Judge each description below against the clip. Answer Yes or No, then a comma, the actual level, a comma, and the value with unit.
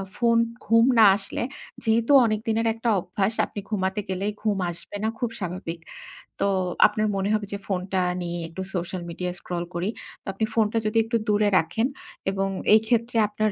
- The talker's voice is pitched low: No, high, 210 Hz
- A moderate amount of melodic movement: Yes, average, 3.2 semitones